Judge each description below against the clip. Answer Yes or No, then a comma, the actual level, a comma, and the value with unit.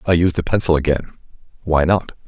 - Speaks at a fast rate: No, average, 185 wpm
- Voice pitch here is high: No, very low, 80 Hz